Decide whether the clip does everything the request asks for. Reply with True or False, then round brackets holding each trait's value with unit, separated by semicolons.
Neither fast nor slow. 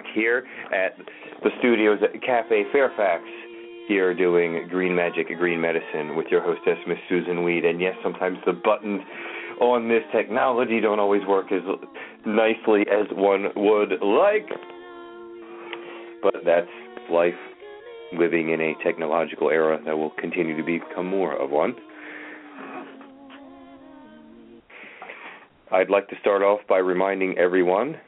False (130 wpm)